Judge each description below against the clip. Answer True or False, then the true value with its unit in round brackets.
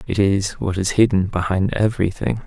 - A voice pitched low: True (100 Hz)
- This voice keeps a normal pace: True (170 wpm)